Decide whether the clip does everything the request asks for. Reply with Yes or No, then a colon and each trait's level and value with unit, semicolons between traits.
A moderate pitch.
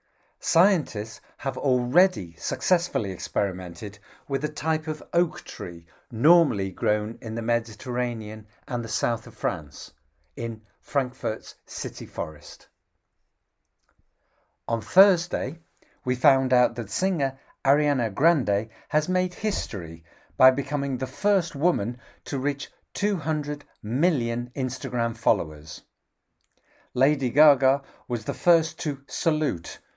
No: low, 130 Hz